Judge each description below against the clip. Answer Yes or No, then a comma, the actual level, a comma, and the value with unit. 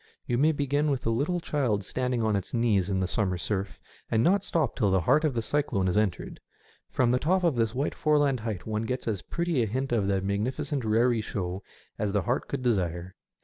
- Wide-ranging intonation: Yes, wide, 5.7 semitones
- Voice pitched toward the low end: Yes, low, 115 Hz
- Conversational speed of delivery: No, fast, 225 wpm